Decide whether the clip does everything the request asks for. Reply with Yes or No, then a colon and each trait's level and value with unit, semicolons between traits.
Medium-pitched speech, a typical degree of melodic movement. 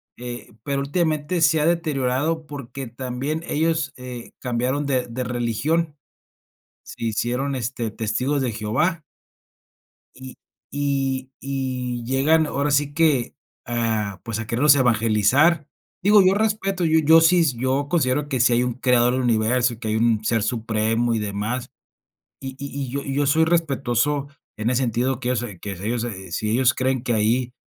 No: low, 130 Hz; average, 3.7 semitones